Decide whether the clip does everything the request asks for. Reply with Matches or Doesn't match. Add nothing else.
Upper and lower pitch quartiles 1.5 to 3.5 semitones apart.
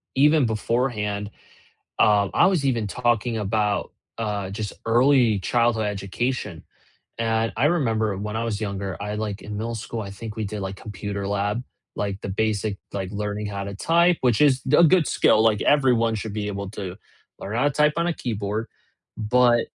Matches